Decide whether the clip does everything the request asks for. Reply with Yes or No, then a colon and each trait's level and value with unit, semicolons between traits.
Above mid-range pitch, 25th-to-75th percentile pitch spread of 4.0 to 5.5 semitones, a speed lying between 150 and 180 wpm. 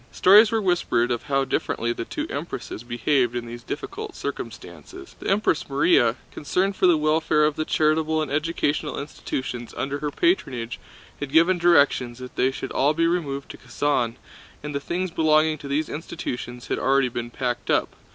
No: medium, 145 Hz; average, 4.7 semitones; average, 175 wpm